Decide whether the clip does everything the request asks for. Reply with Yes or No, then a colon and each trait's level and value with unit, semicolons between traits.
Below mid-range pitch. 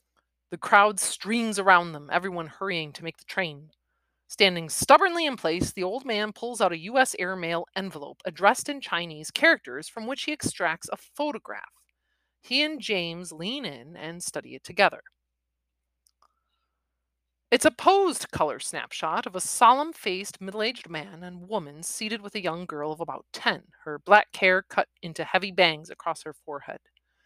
No: medium, 185 Hz